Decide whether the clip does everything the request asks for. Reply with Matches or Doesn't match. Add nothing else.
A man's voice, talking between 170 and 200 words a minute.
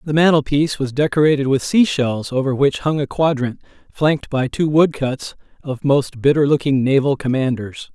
Matches